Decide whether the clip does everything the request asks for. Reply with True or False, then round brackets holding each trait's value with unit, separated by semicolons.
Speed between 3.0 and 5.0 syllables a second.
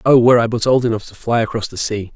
False (6.9 syllables/s)